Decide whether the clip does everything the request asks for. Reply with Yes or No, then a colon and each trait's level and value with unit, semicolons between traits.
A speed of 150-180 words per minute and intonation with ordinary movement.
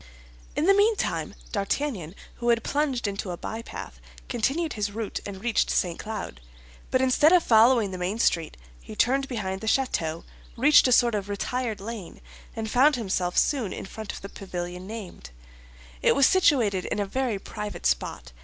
Yes: average, 175 wpm; average, 5.0 semitones